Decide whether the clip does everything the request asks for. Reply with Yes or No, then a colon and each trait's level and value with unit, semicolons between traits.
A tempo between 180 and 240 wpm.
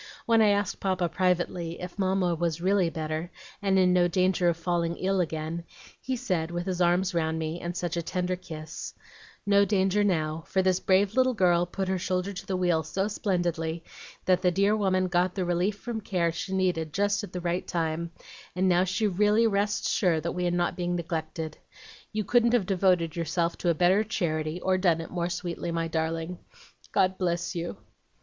Yes: average, 195 wpm